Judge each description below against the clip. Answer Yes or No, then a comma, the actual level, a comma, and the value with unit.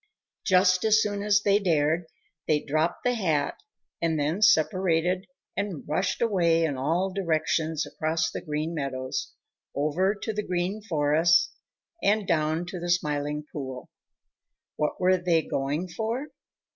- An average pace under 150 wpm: Yes, average, 140 wpm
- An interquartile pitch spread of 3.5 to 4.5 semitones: Yes, average, 4.1 semitones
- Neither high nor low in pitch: Yes, medium, 170 Hz